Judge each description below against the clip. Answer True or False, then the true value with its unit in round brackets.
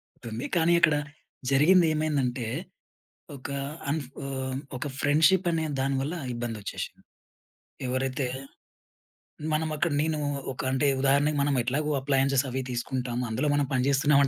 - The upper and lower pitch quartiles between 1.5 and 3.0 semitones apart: True (2.7 semitones)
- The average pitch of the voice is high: False (140 Hz)